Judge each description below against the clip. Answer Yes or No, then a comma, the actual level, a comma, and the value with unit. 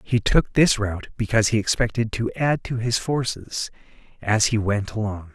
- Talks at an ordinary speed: Yes, average, 180 wpm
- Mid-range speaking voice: No, low, 110 Hz